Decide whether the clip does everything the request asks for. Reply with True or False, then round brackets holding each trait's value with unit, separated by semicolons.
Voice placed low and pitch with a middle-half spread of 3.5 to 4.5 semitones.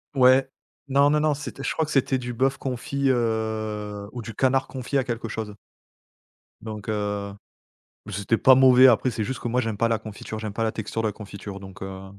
True (115 Hz; 3.8 semitones)